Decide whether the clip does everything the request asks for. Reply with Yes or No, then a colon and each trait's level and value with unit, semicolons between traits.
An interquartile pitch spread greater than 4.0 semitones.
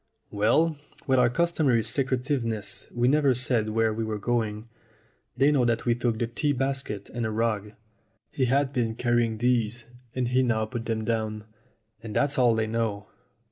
No: average, 2.7 semitones